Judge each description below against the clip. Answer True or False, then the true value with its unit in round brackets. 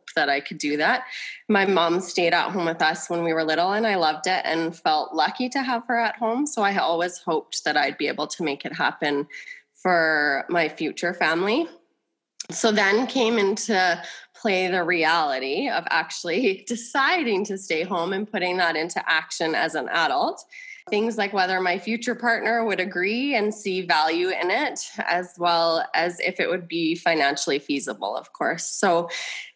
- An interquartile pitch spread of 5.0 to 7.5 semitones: True (5.3 semitones)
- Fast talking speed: False (185 wpm)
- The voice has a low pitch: False (185 Hz)